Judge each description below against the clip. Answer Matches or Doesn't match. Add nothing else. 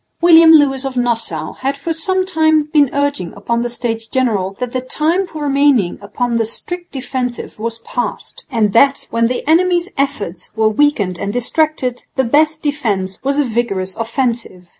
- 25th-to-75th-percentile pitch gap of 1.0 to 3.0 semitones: Doesn't match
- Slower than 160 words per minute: Doesn't match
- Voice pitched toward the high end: Matches